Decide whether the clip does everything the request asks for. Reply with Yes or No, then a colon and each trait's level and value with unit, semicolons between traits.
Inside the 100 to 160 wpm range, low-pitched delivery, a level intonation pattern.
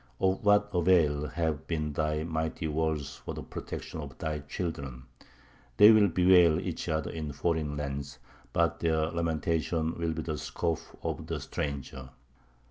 Yes: average, 150 wpm; very low, 80 Hz; narrow, 2.1 semitones